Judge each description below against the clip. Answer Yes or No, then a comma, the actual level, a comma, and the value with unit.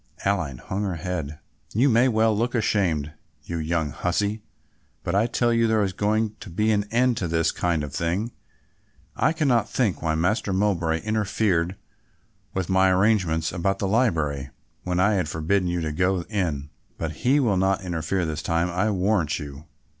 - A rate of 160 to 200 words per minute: Yes, average, 175 wpm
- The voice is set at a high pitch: No, very low, 95 Hz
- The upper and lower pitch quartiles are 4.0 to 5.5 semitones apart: Yes, average, 4.6 semitones